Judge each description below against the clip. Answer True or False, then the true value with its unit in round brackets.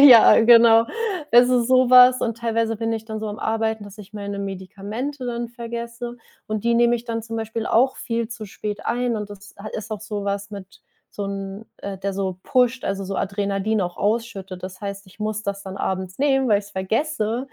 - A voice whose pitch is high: True (220 Hz)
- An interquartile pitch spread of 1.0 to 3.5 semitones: True (2.8 semitones)